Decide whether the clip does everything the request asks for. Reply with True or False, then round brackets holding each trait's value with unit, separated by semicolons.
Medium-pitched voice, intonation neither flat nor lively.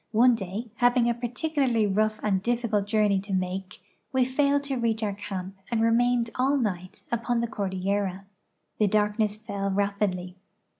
False (215 Hz; 3.3 semitones)